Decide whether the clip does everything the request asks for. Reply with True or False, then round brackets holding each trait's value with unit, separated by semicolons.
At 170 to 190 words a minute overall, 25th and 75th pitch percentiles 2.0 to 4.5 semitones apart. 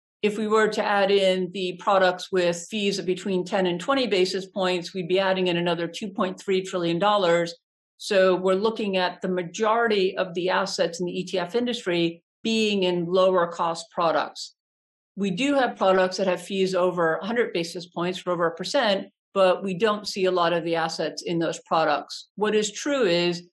True (185 wpm; 2.8 semitones)